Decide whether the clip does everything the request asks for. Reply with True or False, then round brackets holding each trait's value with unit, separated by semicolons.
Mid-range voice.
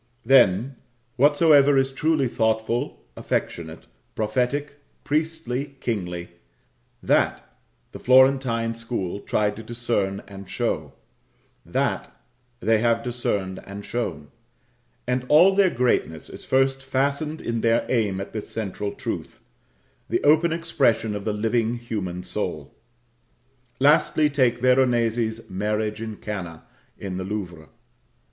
False (115 Hz)